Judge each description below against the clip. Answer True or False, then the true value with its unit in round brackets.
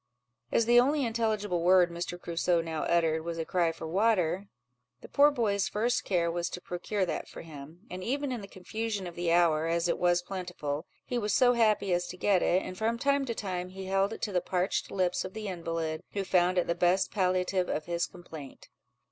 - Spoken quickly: True (215 wpm)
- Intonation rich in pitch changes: False (3.5 semitones)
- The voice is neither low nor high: True (180 Hz)